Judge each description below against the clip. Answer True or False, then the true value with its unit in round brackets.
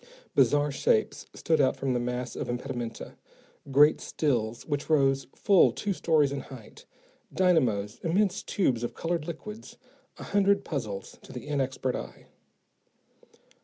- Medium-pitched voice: True (145 Hz)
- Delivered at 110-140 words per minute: True (135 wpm)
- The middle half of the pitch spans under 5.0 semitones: False (5.4 semitones)